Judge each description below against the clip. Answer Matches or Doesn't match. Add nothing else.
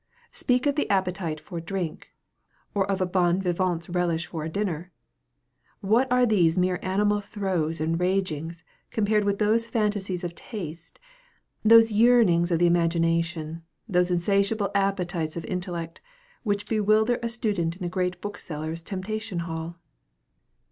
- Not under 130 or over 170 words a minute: Matches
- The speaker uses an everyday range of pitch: Matches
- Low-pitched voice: Doesn't match